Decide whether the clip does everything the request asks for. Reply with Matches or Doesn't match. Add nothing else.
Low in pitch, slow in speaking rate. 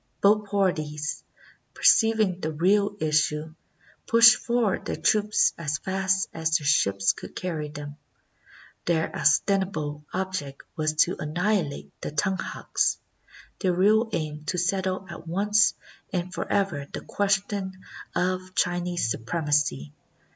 Doesn't match